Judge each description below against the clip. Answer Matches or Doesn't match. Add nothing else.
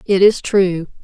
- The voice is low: Doesn't match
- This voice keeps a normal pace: Matches